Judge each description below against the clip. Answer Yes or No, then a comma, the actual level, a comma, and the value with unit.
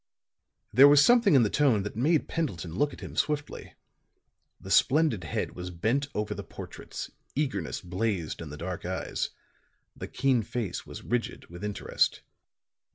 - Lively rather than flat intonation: Yes, wide, 7.7 semitones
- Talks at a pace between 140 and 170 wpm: Yes, average, 160 wpm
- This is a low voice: Yes, low, 110 Hz